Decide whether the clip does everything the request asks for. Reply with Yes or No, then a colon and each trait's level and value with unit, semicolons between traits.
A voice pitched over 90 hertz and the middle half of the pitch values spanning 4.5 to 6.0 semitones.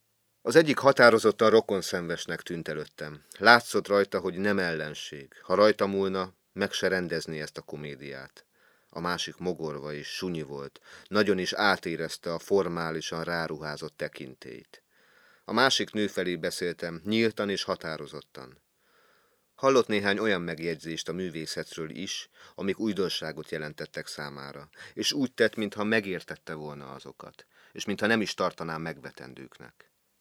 No: very low, 85 Hz; average, 5.1 semitones